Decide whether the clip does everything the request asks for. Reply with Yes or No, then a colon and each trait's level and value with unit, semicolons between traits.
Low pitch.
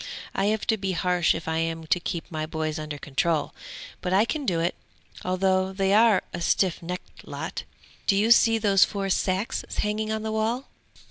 No: high, 190 Hz